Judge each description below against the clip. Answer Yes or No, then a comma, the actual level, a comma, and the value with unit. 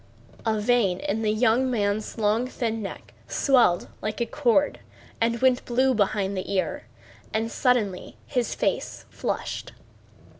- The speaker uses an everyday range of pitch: Yes, average, 3.2 semitones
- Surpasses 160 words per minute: No, average, 140 wpm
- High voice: Yes, high, 225 Hz